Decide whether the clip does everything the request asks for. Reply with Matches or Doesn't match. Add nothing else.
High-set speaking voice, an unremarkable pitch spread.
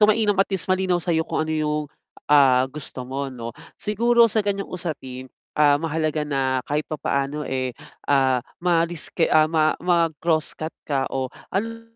Doesn't match